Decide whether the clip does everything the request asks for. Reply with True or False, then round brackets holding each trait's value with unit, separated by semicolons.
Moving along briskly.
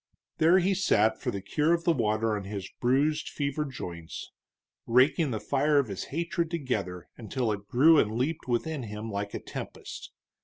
False (180 wpm)